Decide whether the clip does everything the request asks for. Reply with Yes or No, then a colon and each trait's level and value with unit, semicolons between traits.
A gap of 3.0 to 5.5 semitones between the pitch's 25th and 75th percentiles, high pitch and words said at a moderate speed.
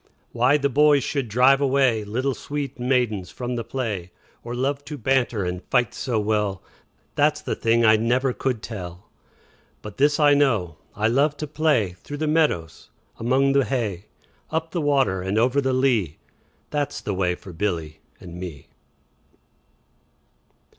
No: average, 5.1 semitones; low, 125 Hz; average, 165 wpm